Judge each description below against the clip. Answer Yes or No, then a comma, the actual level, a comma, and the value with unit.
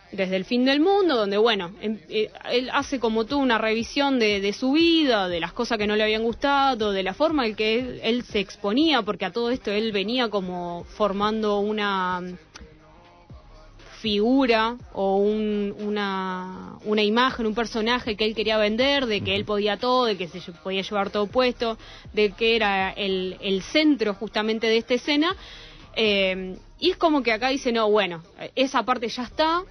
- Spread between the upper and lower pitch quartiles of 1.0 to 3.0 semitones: No, average, 3.5 semitones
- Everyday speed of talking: Yes, average, 180 wpm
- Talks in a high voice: Yes, high, 220 Hz